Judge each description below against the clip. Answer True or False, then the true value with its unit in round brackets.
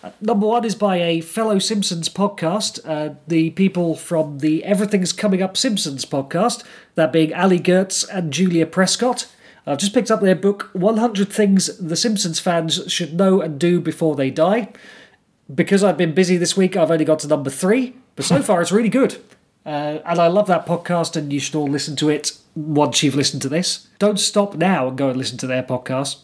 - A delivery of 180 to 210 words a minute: True (205 wpm)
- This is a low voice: False (175 Hz)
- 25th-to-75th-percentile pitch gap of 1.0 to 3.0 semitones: False (4.7 semitones)